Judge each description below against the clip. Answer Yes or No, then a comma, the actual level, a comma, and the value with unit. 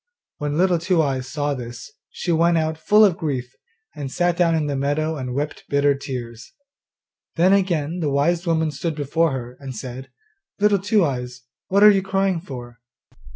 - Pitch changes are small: No, average, 4.5 semitones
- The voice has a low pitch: No, medium, 155 Hz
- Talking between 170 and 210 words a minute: Yes, average, 180 wpm